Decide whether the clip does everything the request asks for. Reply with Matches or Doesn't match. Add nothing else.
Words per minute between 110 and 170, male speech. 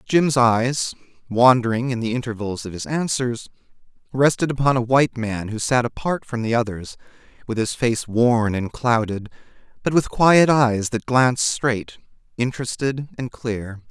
Matches